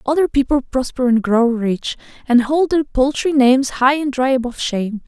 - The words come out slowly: No, average, 190 wpm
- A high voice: Yes, very high, 260 Hz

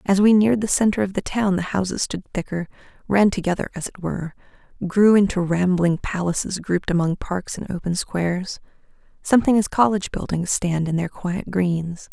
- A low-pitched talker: No, medium, 185 Hz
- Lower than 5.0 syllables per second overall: No, 5.4 syllables/s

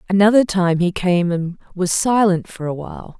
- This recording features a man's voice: No, female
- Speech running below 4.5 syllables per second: No, 5.0 syllables/s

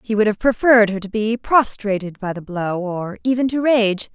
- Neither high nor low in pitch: No, high, 215 Hz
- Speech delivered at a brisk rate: Yes, fast, 215 wpm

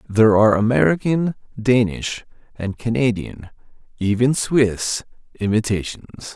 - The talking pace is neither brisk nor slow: No, slow, 65 wpm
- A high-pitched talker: No, low, 115 Hz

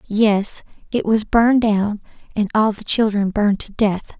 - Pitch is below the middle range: No, high, 210 Hz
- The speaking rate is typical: Yes, average, 170 wpm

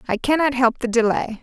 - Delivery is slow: No, fast, 210 wpm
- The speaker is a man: No, female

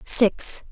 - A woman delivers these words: Yes, female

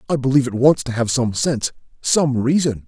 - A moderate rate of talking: No, fast, 210 wpm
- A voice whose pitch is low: Yes, low, 130 Hz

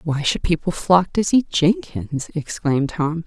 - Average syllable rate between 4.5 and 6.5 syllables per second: No, 4.2 syllables/s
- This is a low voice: No, medium, 170 Hz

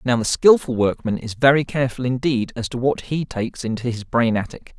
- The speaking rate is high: Yes, fast, 215 wpm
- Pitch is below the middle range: Yes, low, 125 Hz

